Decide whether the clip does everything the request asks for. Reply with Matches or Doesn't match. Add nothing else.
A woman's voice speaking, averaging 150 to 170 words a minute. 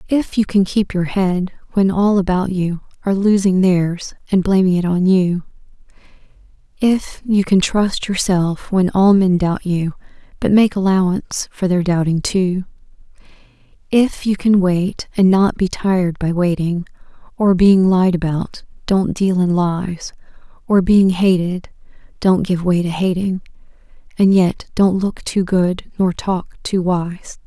Matches